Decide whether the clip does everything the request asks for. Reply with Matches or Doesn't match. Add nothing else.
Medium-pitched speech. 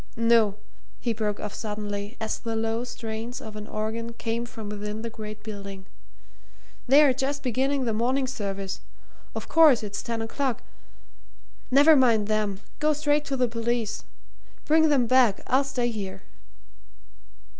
Doesn't match